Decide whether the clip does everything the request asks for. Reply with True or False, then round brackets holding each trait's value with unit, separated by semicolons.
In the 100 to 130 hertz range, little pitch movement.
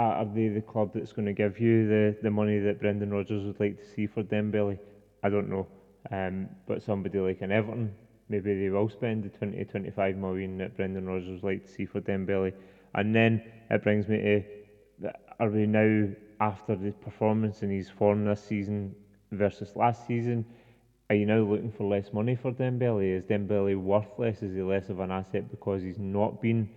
True (105 Hz; 1.7 semitones)